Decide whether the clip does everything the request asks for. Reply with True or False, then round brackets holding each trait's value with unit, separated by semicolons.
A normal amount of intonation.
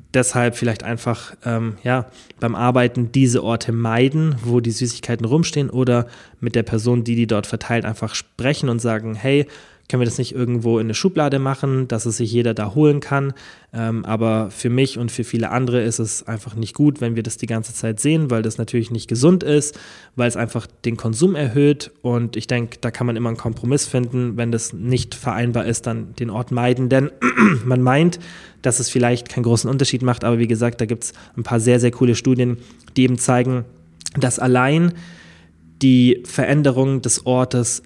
False (2.0 semitones)